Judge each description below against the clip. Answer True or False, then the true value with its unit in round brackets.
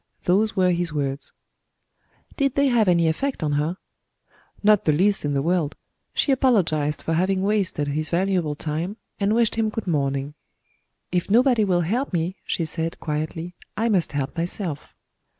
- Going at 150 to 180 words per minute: True (165 wpm)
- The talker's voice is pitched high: False (175 Hz)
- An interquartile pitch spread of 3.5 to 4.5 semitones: False (5.3 semitones)